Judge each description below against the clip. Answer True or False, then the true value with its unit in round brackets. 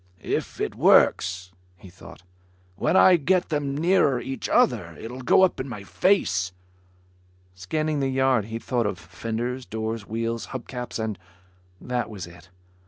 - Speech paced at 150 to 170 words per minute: True (155 wpm)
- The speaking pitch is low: True (120 Hz)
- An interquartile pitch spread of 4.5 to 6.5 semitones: True (4.9 semitones)